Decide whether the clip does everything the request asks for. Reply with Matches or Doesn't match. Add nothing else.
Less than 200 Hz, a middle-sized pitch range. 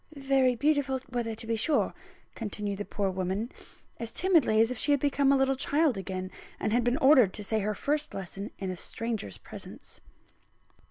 Doesn't match